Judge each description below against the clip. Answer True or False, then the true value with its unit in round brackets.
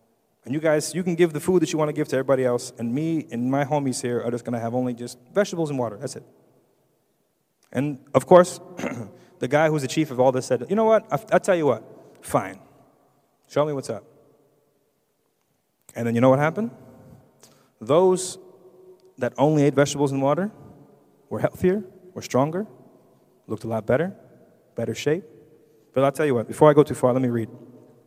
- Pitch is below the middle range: False (145 Hz)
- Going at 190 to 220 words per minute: True (200 wpm)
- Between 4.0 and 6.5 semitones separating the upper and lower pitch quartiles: True (4.4 semitones)